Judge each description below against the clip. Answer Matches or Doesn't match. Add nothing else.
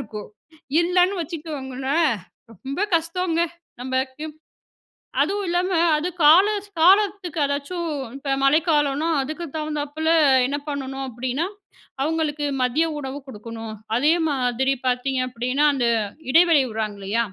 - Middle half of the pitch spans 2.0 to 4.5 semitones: Matches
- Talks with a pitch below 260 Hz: Doesn't match